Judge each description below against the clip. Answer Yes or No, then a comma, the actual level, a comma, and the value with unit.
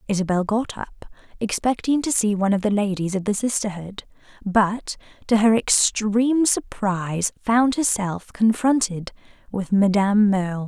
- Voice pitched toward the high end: Yes, high, 210 Hz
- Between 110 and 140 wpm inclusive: Yes, slow, 135 wpm